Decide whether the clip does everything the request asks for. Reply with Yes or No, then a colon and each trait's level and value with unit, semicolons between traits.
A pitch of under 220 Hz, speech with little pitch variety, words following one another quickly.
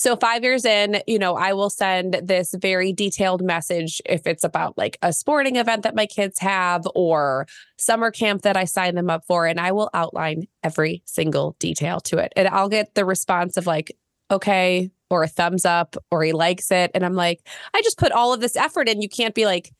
No: high, 190 Hz; average, 3.3 semitones; fast, 220 wpm